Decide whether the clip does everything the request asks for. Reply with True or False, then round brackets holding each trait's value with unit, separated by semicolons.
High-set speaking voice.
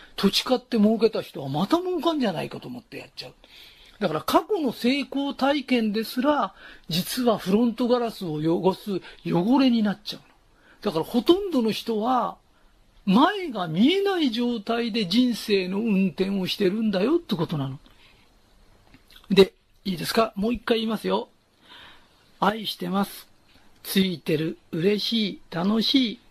True (215 Hz)